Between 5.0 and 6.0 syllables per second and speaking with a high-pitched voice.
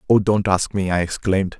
No: 5.7 syllables/s; very low, 95 Hz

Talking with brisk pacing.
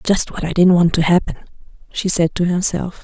Yes: fast, 220 wpm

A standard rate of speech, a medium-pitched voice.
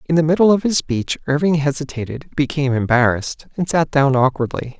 Yes: average, 175 wpm; medium, 145 Hz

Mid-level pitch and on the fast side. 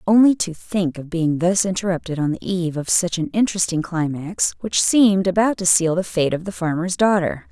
Yes: medium, 180 Hz; fast, 210 wpm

